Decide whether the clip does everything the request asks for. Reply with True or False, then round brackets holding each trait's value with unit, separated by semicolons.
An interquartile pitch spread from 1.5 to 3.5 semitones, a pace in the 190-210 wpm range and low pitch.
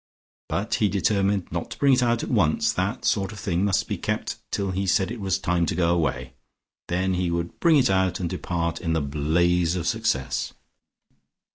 True (2.8 semitones; 205 wpm; 90 Hz)